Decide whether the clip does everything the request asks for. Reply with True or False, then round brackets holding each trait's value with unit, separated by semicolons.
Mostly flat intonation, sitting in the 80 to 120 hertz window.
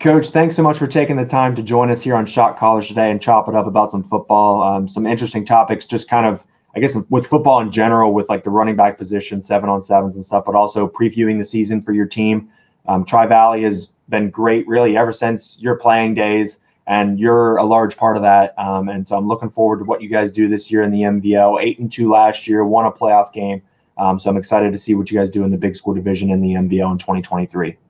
True (2.1 semitones; 105 Hz)